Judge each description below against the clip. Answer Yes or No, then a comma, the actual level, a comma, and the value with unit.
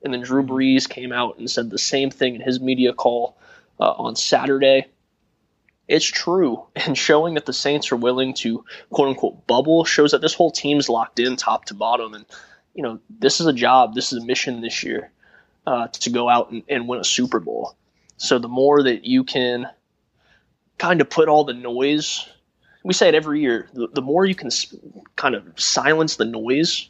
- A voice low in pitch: Yes, low, 130 Hz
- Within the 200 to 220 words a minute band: Yes, fast, 205 wpm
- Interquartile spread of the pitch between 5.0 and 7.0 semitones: No, average, 3.5 semitones